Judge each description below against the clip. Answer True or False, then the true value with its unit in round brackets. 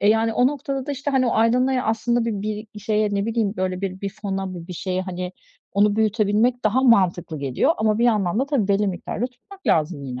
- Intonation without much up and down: False (4.3 semitones)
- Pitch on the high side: True (215 Hz)